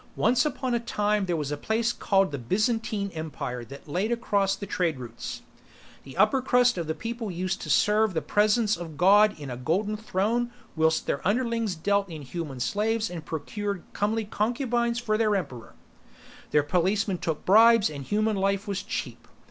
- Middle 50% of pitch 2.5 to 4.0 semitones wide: No, average, 5.2 semitones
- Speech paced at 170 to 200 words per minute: Yes, average, 175 wpm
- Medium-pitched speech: No, high, 200 Hz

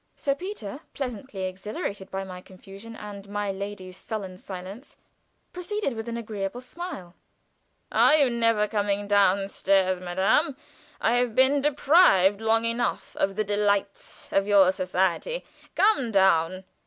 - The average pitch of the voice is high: Yes, high, 205 Hz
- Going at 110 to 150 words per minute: Yes, slow, 135 wpm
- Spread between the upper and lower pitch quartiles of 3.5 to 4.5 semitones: Yes, average, 4.0 semitones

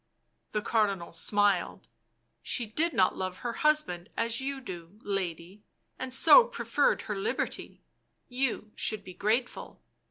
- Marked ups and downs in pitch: Yes, wide, 5.8 semitones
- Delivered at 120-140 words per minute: Yes, slow, 135 wpm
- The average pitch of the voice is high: Yes, high, 215 Hz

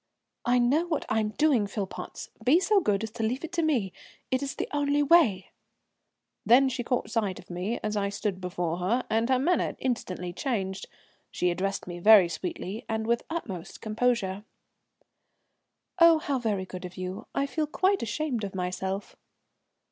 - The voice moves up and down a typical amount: No, wide, 6.3 semitones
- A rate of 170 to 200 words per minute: Yes, average, 180 wpm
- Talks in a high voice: Yes, high, 220 Hz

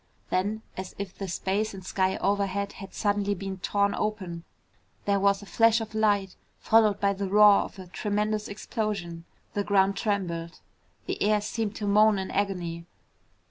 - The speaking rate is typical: Yes, average, 165 wpm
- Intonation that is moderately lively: No, narrow, 1.7 semitones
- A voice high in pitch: Yes, high, 200 Hz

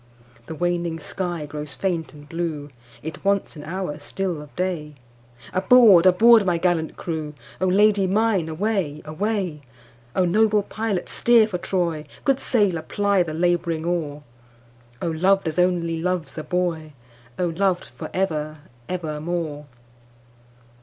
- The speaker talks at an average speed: No, slow, 120 wpm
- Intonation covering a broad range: No, average, 3.9 semitones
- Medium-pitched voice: Yes, medium, 170 Hz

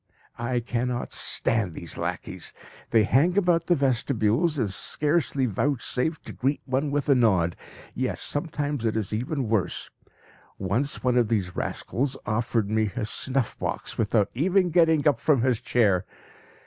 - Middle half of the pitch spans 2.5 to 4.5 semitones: No, average, 4.9 semitones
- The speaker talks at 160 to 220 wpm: No, average, 150 wpm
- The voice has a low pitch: Yes, low, 125 Hz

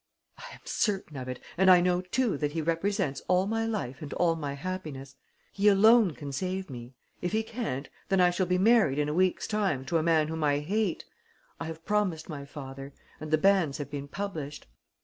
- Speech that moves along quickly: Yes, fast, 210 wpm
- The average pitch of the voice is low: No, medium, 165 Hz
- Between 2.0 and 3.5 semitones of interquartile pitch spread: No, average, 5.1 semitones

